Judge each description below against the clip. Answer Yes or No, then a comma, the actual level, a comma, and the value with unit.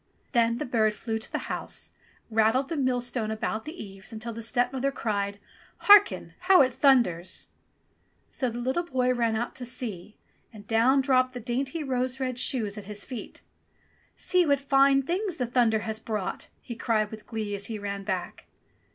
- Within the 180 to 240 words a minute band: Yes, average, 185 wpm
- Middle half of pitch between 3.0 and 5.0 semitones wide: Yes, average, 3.4 semitones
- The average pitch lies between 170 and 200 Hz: No, high, 240 Hz